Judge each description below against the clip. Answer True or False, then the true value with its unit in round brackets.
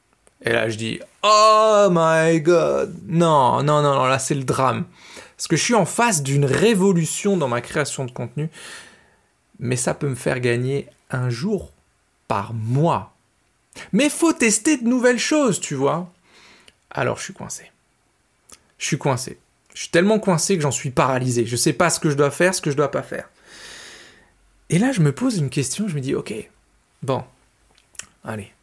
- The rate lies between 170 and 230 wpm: True (190 wpm)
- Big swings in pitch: True (6.7 semitones)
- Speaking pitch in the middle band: True (160 Hz)